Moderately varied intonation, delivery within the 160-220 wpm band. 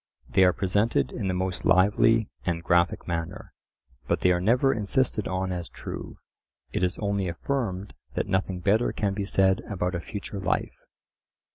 No: narrow, 2.2 semitones; average, 165 wpm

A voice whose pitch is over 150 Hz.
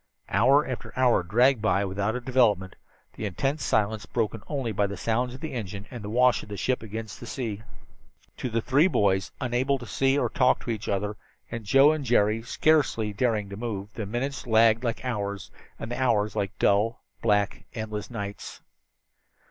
No: low, 115 Hz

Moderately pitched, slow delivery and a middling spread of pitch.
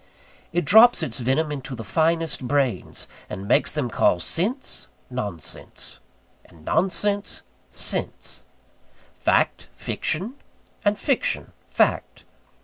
No: medium, 155 Hz; slow, 105 wpm; wide, 7.7 semitones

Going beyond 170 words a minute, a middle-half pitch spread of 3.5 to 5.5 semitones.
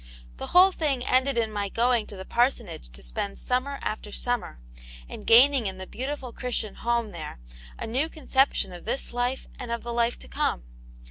Yes: average, 190 wpm; average, 4.1 semitones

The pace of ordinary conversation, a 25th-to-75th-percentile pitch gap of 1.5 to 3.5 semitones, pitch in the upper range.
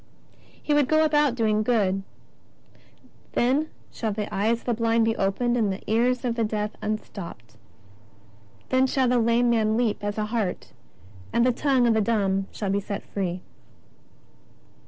Yes: average, 170 wpm; average, 3.0 semitones; high, 225 Hz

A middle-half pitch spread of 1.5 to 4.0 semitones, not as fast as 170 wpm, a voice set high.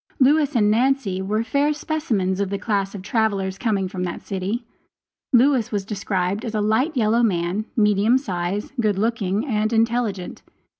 Yes: average, 3.6 semitones; average, 160 wpm; high, 215 Hz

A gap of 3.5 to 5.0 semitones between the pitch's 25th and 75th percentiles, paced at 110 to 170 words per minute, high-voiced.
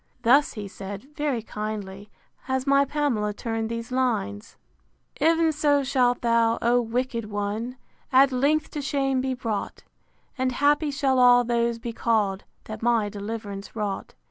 Yes: average, 4.0 semitones; average, 150 wpm; high, 240 Hz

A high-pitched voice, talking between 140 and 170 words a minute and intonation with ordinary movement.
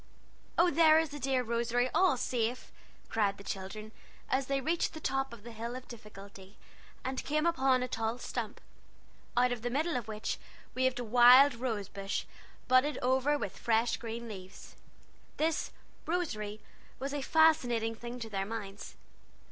Yes: high, 245 Hz; average, 165 wpm; average, 3.6 semitones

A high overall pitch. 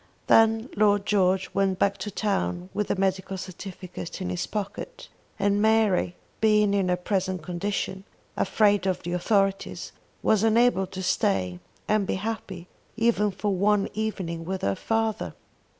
Yes: high, 195 Hz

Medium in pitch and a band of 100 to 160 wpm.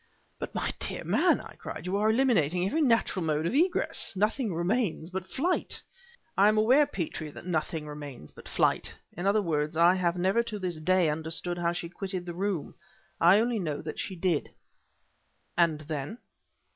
No: medium, 180 Hz; average, 180 wpm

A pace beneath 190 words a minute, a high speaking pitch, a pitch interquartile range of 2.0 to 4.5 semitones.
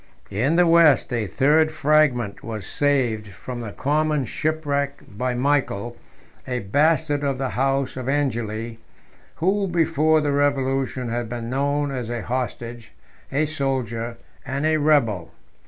No: average, 140 wpm; low, 135 Hz; average, 3.7 semitones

